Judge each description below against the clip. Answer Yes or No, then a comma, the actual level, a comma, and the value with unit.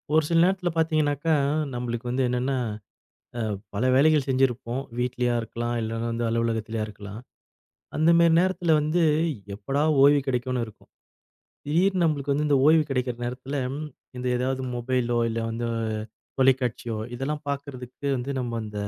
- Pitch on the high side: No, low, 130 Hz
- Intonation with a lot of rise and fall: No, average, 3.7 semitones